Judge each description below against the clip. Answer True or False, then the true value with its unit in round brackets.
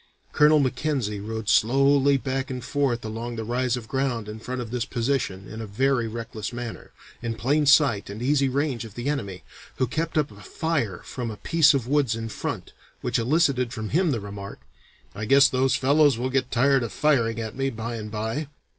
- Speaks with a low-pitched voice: True (125 Hz)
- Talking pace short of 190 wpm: False (200 wpm)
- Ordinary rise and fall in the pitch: True (3.7 semitones)